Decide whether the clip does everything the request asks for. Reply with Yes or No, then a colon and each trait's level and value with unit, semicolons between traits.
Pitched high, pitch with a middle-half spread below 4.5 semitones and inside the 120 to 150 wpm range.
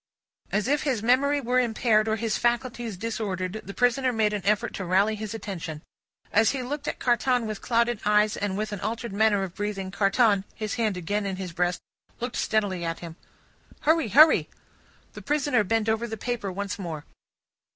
No: high, 215 Hz; average, 3.4 semitones; average, 185 wpm